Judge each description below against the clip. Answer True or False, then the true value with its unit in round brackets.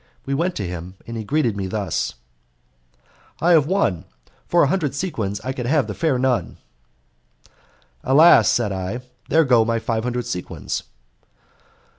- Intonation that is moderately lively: False (6.3 semitones)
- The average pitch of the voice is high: False (125 Hz)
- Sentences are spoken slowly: False (155 wpm)